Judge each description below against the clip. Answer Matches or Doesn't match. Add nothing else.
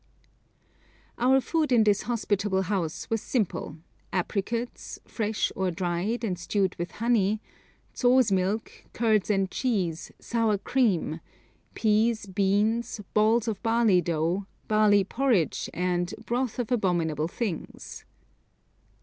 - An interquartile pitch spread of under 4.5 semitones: Matches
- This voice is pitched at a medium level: Doesn't match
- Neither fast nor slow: Doesn't match